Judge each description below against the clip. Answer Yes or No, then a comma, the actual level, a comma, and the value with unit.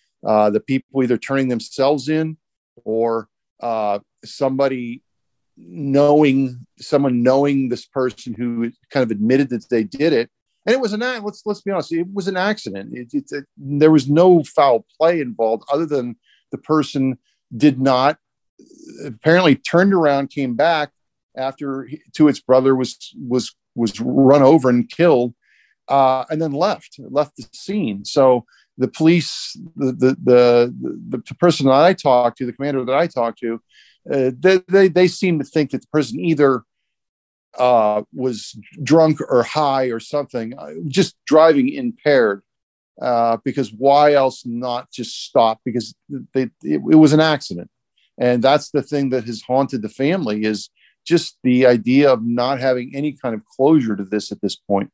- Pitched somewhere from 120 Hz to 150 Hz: Yes, low, 135 Hz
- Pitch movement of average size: Yes, average, 4.1 semitones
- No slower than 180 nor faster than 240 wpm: No, average, 170 wpm